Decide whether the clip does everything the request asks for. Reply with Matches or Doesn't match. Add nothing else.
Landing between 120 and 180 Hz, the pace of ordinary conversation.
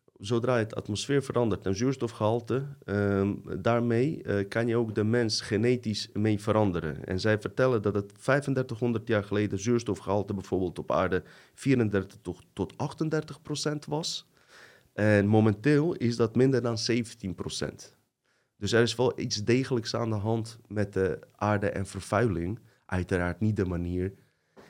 Doesn't match